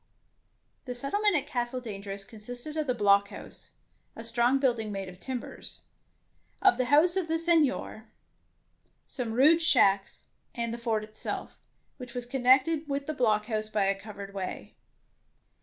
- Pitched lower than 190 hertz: No, high, 245 Hz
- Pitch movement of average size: Yes, average, 4.8 semitones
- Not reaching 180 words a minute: Yes, average, 145 wpm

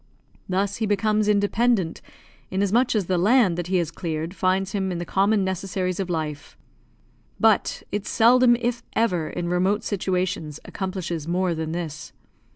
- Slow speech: No, average, 155 wpm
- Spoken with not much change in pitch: No, average, 3.1 semitones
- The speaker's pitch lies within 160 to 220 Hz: Yes, high, 190 Hz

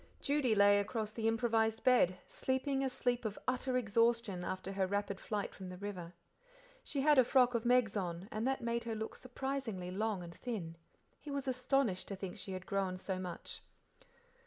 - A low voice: No, high, 220 Hz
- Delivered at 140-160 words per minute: No, average, 180 wpm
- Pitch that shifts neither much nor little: Yes, average, 4.7 semitones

